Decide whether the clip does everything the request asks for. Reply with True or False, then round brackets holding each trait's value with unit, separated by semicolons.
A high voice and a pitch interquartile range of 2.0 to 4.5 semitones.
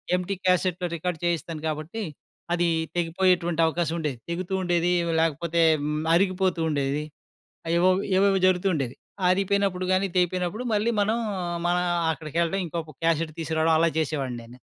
False (175 Hz; 2.5 semitones)